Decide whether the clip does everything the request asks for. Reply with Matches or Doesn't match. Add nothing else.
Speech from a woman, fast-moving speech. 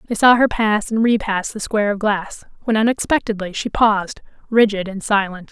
Doesn't match